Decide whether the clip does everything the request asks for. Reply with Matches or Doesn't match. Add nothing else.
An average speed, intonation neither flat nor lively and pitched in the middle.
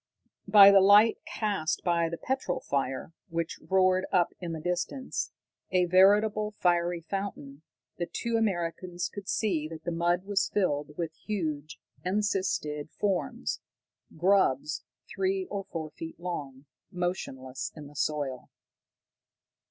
Doesn't match